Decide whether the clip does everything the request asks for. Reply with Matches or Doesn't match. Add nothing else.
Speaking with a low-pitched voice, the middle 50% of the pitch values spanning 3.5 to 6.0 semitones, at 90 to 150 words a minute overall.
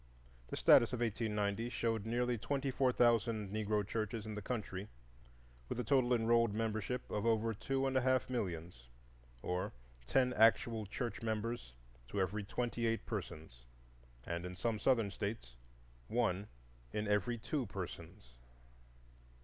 Doesn't match